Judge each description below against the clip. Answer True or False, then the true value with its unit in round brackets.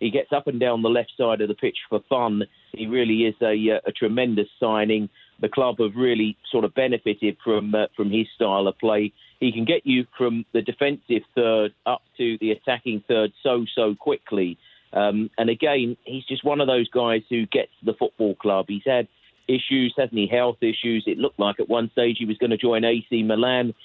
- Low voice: True (115 Hz)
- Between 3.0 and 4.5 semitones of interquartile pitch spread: False (2.4 semitones)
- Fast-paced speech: True (215 wpm)